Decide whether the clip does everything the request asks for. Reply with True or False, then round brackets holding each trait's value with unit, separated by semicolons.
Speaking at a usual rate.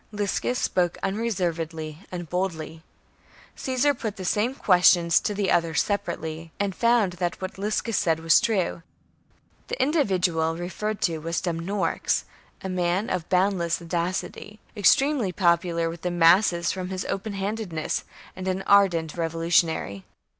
False (130 wpm)